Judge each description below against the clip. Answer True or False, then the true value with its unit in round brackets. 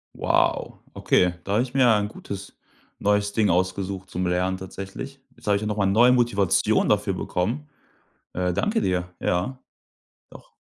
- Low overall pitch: True (100 Hz)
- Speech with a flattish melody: False (3.0 semitones)